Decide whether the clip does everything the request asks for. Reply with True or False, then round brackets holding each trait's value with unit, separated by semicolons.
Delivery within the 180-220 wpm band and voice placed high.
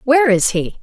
True (215 wpm; 245 Hz)